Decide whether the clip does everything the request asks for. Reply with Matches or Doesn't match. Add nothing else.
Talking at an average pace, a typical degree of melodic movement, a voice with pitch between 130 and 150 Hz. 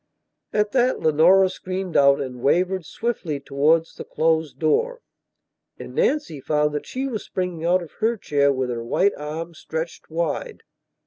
Doesn't match